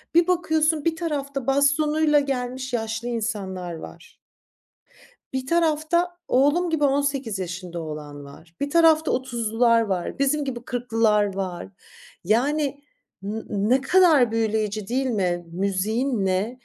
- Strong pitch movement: Yes, wide, 5.9 semitones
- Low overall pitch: No, high, 245 Hz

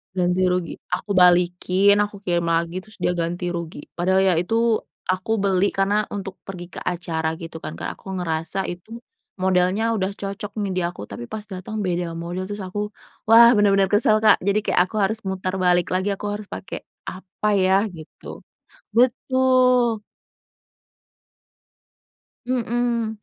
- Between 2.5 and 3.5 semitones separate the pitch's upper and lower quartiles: Yes, average, 3.1 semitones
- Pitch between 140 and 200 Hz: Yes, high, 190 Hz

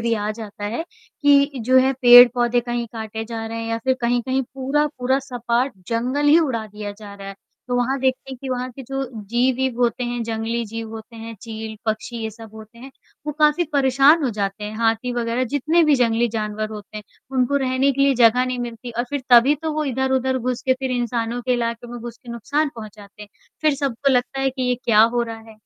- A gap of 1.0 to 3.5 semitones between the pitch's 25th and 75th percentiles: Yes, average, 2.8 semitones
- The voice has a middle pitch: No, high, 245 Hz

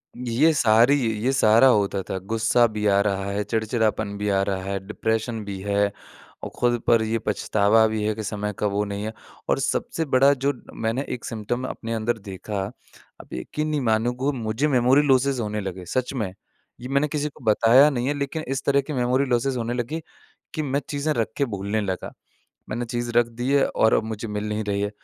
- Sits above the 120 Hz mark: No, low, 115 Hz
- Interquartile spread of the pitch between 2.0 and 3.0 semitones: No, average, 3.7 semitones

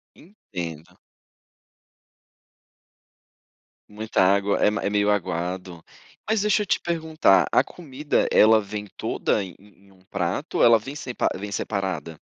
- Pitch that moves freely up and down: Yes, wide, 5.8 semitones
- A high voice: No, low, 105 Hz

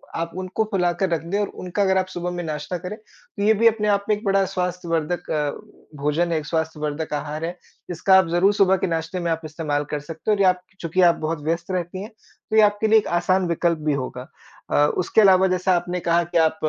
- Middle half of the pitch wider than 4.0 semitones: No, average, 2.8 semitones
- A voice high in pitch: No, medium, 175 Hz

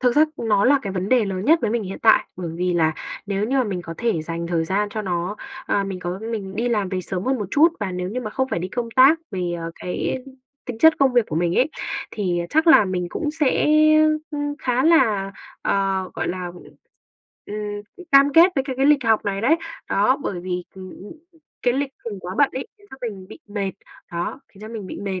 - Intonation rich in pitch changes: Yes, wide, 5.8 semitones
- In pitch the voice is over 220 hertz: No, high, 205 Hz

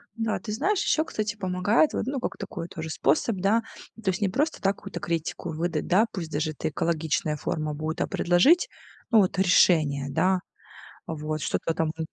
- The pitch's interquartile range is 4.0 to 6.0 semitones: Yes, average, 5.0 semitones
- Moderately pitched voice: Yes, medium, 180 Hz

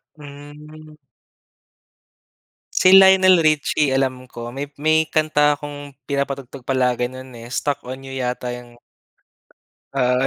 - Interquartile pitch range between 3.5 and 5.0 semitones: No, average, 3.0 semitones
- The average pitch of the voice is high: No, medium, 140 Hz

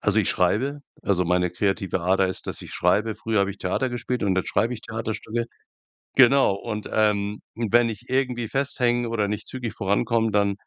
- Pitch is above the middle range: No, low, 110 Hz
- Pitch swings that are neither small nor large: Yes, average, 3.3 semitones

